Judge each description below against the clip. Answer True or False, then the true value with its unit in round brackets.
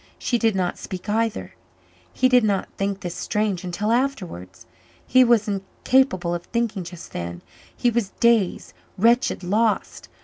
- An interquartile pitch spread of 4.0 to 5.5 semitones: True (4.4 semitones)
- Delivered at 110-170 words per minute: True (145 wpm)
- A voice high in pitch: True (210 Hz)